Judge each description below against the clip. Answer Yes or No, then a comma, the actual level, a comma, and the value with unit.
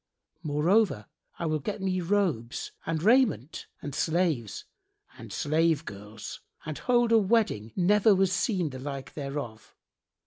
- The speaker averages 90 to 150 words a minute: Yes, slow, 135 wpm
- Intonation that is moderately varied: No, wide, 6.2 semitones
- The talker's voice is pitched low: No, medium, 165 Hz